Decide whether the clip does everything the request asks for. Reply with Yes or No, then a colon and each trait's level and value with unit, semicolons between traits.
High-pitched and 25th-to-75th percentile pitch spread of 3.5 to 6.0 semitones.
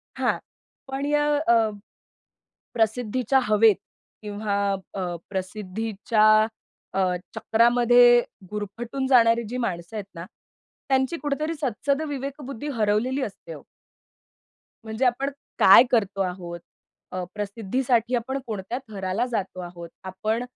Yes: high, 225 Hz; average, 4.0 semitones